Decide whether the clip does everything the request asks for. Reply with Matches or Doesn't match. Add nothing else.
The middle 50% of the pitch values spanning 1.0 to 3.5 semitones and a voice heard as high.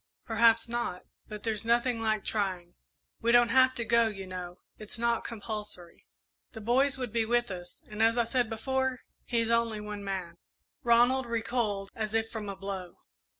Matches